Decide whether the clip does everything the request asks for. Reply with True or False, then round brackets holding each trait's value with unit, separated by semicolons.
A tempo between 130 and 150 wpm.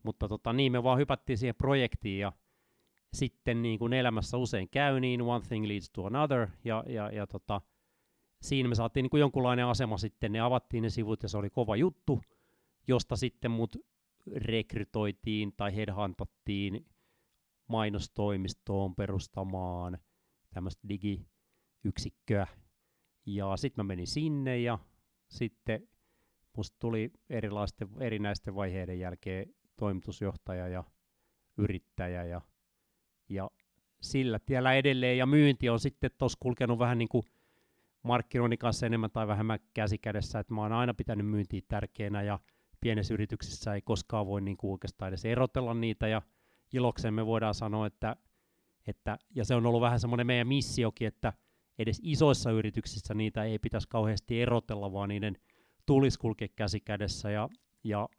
True (140 wpm)